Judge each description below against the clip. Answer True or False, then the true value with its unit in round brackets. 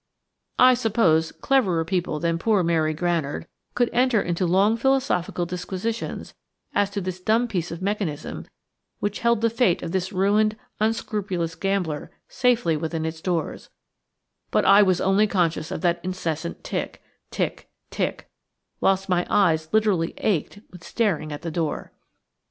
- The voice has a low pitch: False (185 Hz)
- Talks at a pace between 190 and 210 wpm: False (145 wpm)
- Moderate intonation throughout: True (4.2 semitones)